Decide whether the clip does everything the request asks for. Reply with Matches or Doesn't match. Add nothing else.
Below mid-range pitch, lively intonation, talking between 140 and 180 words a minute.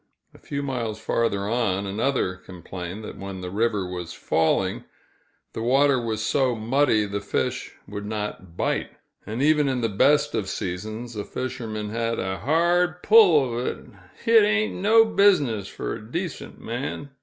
Matches